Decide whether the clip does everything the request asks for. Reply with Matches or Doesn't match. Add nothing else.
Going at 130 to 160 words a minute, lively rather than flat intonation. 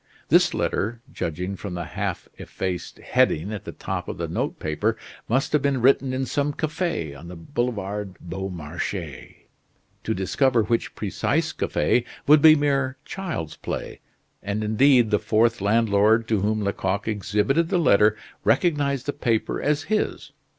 Matches